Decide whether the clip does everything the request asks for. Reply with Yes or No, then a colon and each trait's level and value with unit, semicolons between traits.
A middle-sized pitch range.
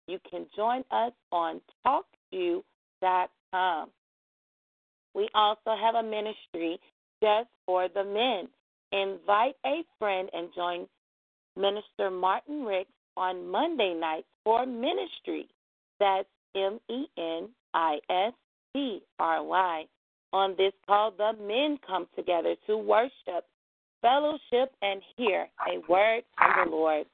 Yes: average, 4.3 semitones